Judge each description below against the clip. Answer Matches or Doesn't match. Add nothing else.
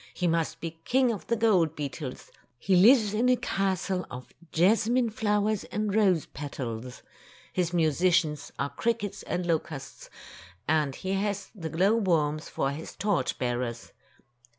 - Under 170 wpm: Matches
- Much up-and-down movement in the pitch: Matches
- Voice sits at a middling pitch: Matches